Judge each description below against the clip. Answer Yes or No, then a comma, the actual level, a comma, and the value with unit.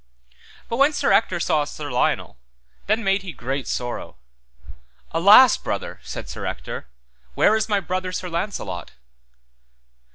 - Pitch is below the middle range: No, medium, 185 Hz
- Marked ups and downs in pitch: Yes, wide, 6.2 semitones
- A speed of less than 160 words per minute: Yes, slow, 135 wpm